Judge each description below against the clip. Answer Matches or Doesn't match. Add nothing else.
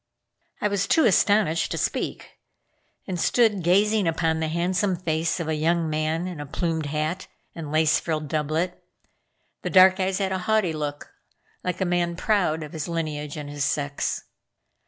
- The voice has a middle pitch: Matches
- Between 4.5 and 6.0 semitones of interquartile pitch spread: Doesn't match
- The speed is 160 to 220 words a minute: Matches